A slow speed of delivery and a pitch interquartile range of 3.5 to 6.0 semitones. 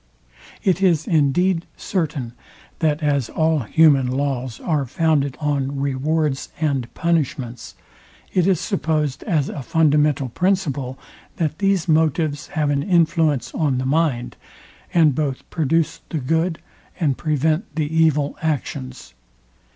No: slow, 125 wpm; average, 2.9 semitones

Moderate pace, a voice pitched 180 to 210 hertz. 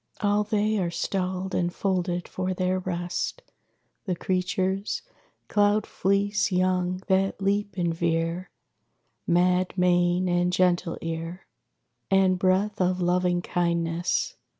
No: slow, 115 wpm; medium, 185 Hz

